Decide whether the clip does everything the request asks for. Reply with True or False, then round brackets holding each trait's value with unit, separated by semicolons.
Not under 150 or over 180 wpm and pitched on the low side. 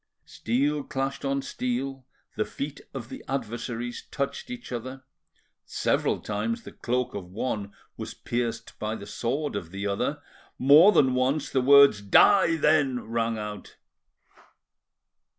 False (135 wpm; 125 Hz)